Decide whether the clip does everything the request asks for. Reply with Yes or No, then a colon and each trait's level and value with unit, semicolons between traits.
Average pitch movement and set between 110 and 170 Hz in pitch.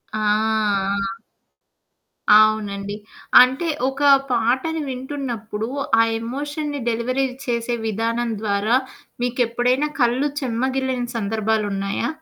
No: average, 3.1 semitones; high, 240 Hz